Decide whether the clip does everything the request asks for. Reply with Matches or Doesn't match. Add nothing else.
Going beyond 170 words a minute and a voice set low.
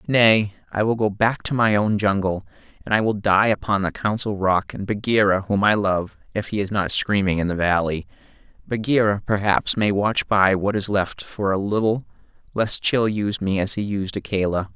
Matches